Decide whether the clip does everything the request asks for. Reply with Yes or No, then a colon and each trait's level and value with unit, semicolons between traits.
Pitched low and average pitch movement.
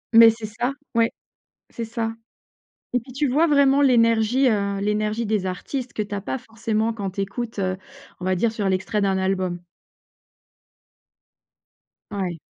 No: high, 220 Hz; average, 3.1 semitones